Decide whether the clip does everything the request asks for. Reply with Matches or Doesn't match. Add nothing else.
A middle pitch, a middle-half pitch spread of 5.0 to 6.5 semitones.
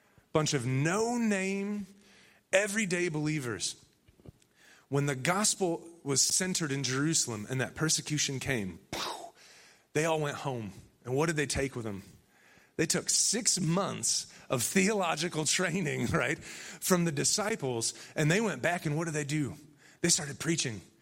Matches